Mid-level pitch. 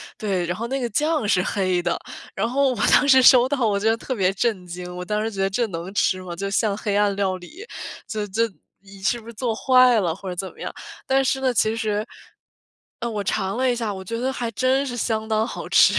No: high, 215 Hz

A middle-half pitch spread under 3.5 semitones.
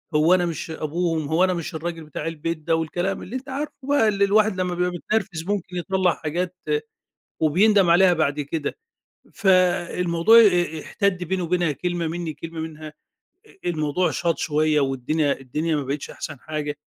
Yes: average, 2.8 semitones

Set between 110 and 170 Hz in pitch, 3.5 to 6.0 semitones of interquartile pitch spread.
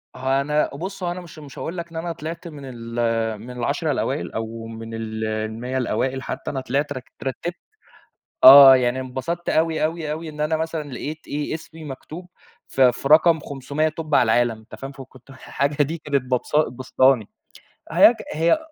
Yes: medium, 140 Hz; average, 4.1 semitones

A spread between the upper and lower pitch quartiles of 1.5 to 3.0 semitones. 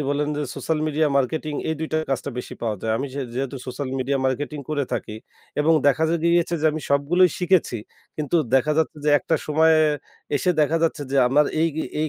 Yes: narrow, 2.6 semitones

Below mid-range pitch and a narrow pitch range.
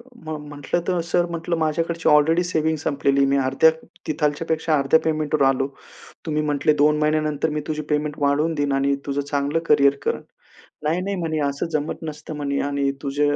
No: medium, 150 Hz; narrow, 2.1 semitones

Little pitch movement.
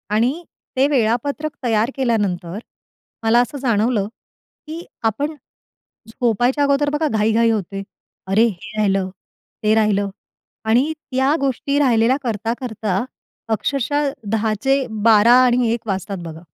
No: average, 4.1 semitones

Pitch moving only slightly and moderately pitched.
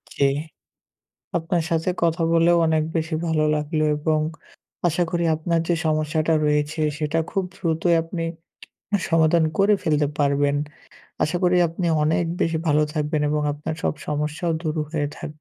Yes: narrow, 1.8 semitones; medium, 160 Hz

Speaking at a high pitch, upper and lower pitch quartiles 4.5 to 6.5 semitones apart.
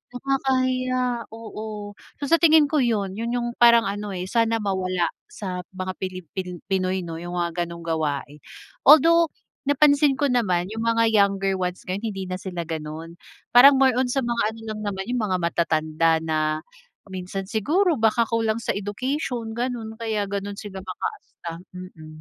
Yes: high, 205 Hz; average, 4.9 semitones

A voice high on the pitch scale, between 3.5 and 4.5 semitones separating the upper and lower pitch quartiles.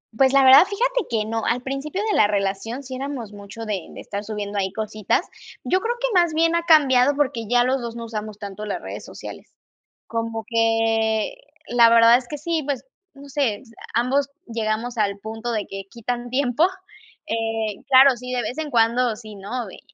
Yes: high, 235 Hz; average, 3.9 semitones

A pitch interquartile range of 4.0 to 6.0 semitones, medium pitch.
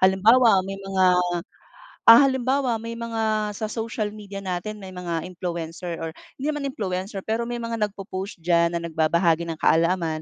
No: average, 4.5 semitones; high, 195 Hz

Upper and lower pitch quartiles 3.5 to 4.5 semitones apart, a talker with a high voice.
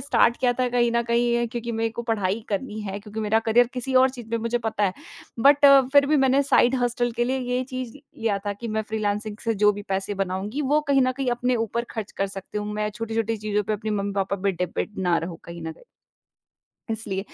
No: average, 3.1 semitones; high, 225 Hz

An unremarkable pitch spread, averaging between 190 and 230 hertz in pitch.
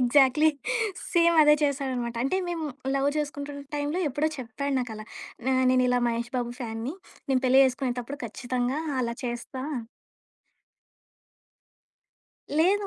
No: average, 3.0 semitones; very high, 260 Hz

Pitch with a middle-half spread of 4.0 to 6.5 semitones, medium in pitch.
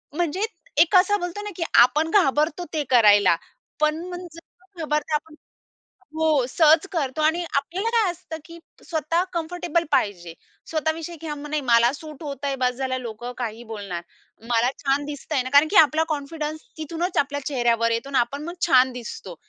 No: average, 4.5 semitones; very high, 300 Hz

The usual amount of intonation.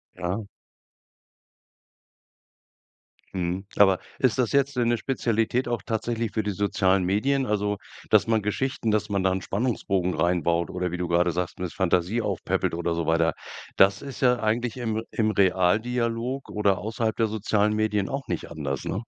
Yes: average, 4.1 semitones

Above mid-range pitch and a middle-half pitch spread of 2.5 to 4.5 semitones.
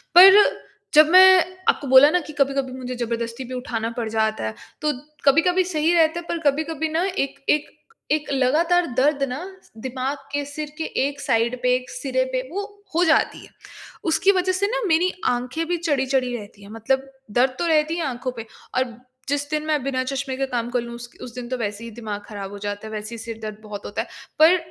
No: very high, 270 Hz; average, 4.9 semitones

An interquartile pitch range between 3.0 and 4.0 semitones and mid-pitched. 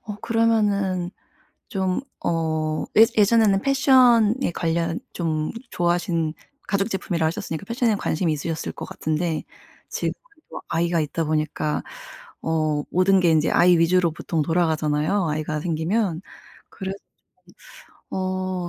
Yes: average, 3.7 semitones; medium, 175 Hz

